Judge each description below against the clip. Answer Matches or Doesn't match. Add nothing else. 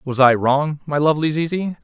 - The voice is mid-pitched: Matches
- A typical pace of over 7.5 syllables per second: Doesn't match